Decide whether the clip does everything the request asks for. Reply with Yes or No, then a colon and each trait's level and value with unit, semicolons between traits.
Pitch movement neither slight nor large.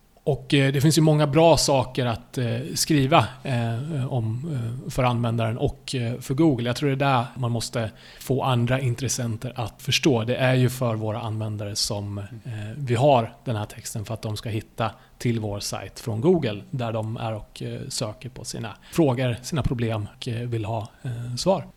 Yes: average, 3.2 semitones